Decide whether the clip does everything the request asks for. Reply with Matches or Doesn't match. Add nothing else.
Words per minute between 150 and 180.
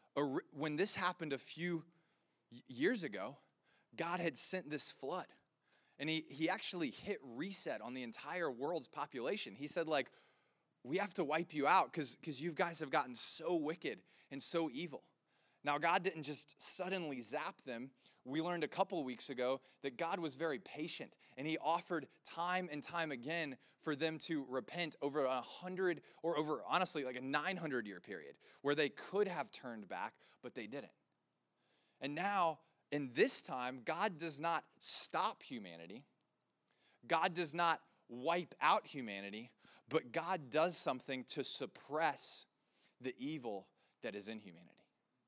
Matches